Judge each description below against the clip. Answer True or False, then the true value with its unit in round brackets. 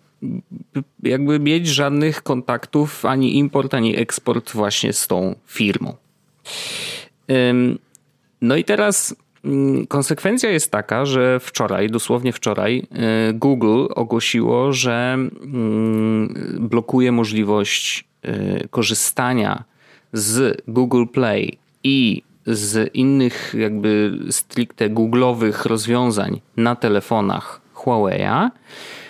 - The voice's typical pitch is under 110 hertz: False (125 Hz)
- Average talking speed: False (85 wpm)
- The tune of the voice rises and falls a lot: False (3.7 semitones)